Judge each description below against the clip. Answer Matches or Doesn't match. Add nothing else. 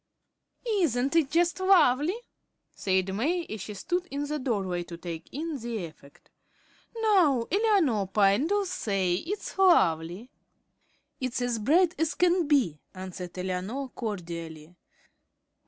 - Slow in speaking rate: Matches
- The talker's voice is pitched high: Matches